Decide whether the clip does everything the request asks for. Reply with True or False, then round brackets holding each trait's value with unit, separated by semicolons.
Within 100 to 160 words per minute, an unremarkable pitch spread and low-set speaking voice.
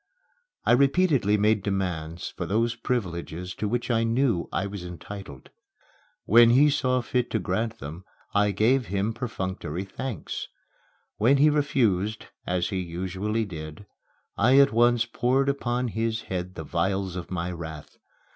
True (145 wpm; 4.9 semitones; 105 Hz)